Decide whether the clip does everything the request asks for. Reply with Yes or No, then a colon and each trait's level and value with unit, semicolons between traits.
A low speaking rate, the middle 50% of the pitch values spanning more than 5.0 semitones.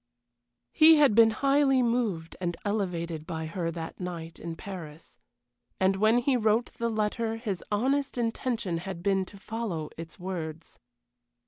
No: average, 145 wpm; wide, 5.5 semitones